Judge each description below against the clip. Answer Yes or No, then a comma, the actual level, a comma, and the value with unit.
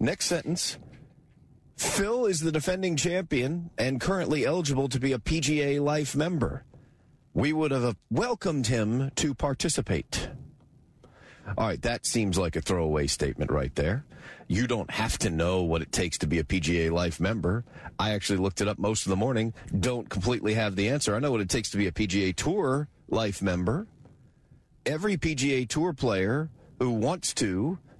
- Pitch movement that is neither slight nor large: No, wide, 7.2 semitones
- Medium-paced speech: Yes, average, 170 wpm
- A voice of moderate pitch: No, low, 125 Hz